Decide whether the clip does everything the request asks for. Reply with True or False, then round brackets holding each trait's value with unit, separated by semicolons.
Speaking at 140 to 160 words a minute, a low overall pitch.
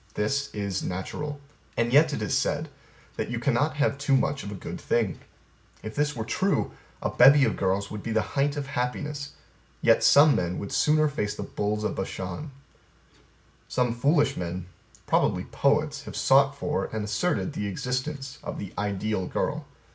False (170 wpm; 125 Hz)